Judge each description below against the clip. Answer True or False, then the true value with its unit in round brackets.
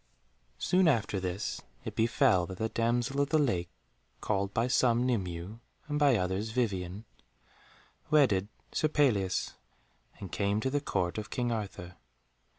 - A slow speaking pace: False (145 wpm)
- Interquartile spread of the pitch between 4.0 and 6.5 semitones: True (5.2 semitones)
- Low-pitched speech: True (110 Hz)